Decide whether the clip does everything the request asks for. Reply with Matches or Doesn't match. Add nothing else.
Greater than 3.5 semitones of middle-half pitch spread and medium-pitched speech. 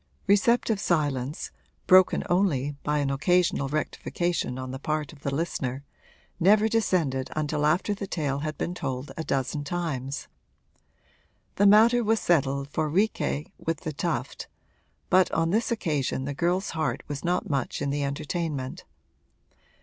Matches